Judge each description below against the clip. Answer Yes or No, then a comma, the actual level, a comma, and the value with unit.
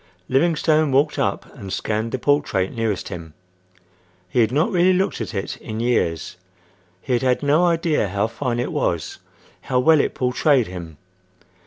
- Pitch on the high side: No, low, 125 Hz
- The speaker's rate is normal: Yes, average, 165 wpm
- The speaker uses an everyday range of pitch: No, wide, 6.4 semitones